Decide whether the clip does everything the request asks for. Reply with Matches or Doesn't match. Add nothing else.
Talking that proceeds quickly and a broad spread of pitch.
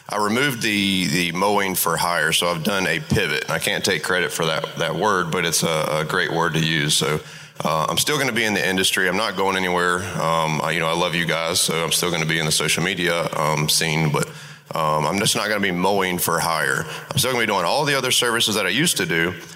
Doesn't match